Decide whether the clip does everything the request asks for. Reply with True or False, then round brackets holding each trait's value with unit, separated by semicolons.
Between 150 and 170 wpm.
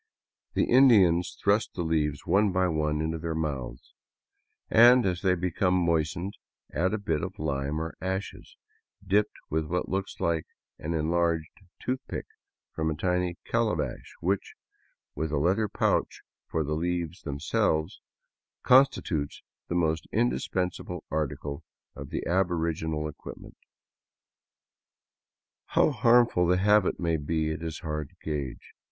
False (135 wpm)